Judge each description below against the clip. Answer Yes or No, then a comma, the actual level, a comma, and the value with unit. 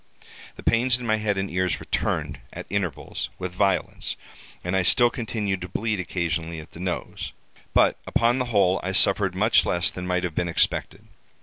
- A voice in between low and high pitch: No, very low, 95 Hz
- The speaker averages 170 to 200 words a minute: Yes, average, 185 wpm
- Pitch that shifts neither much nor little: Yes, average, 3.3 semitones